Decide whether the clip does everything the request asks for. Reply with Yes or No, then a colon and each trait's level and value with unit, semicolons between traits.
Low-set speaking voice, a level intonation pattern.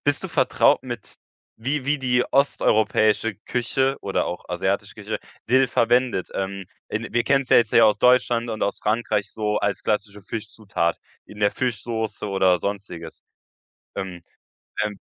No: low, 110 Hz; average, 3.6 semitones